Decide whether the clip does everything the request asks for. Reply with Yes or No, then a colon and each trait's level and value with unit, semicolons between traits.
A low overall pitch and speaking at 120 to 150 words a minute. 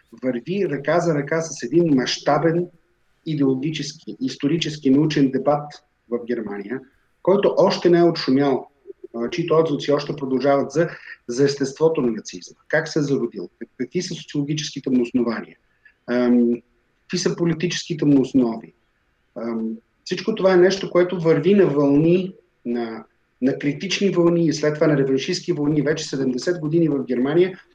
No: medium, 145 Hz; average, 140 wpm